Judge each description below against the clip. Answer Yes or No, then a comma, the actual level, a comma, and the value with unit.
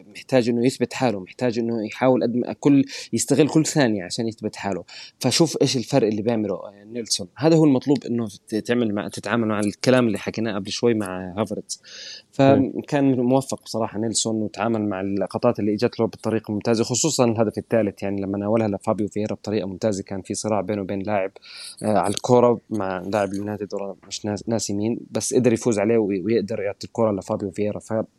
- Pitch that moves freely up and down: No, average, 2.9 semitones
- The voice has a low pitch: Yes, low, 110 Hz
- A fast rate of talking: Yes, fast, 175 wpm